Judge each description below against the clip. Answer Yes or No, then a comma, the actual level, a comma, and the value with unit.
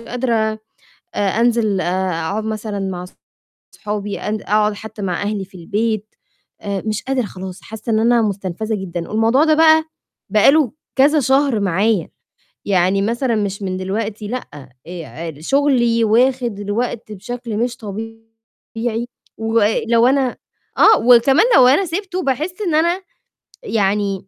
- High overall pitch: Yes, high, 220 Hz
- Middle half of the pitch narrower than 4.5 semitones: Yes, average, 3.6 semitones